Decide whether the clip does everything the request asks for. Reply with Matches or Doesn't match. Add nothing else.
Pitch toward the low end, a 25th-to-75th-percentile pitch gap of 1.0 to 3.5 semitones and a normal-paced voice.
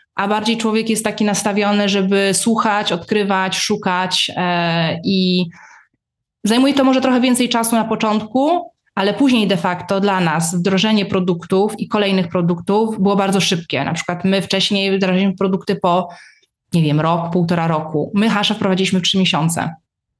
Doesn't match